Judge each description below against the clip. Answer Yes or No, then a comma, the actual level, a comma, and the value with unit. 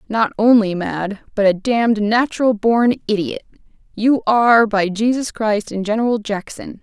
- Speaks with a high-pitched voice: Yes, high, 220 Hz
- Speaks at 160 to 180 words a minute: No, average, 150 wpm